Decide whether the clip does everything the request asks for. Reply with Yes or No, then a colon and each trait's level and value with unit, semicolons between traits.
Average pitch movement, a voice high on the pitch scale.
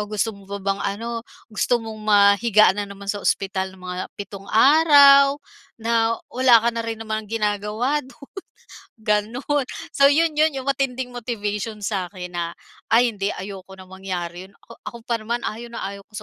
Yes: average, 3.3 semitones; high, 215 Hz